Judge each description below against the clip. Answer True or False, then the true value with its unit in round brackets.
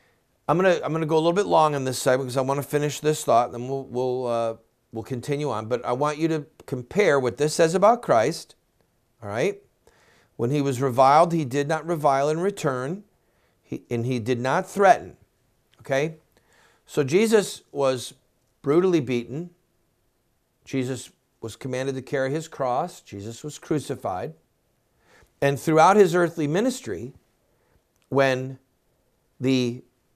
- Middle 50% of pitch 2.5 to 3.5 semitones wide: False (4.0 semitones)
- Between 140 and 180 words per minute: True (155 wpm)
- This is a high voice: False (140 Hz)